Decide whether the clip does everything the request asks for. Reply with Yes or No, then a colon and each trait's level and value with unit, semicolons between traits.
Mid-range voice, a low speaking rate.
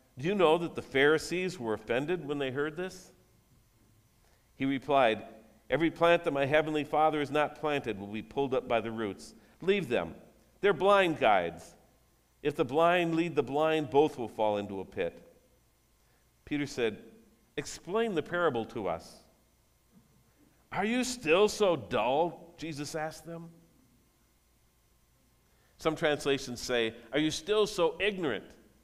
No: medium, 150 Hz; average, 145 wpm